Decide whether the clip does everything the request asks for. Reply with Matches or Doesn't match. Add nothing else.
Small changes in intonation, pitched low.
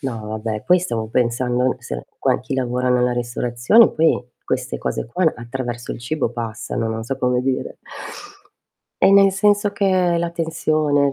Doesn't match